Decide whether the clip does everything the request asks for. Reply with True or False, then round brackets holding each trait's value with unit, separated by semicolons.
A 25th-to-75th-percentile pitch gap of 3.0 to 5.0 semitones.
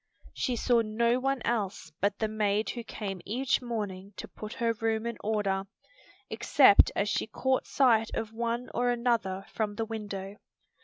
False (2.5 semitones)